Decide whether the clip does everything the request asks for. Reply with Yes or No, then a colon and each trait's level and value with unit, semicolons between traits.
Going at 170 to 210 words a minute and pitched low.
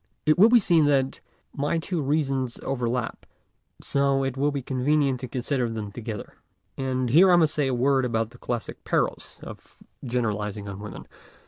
Yes: average, 180 wpm; low, 130 Hz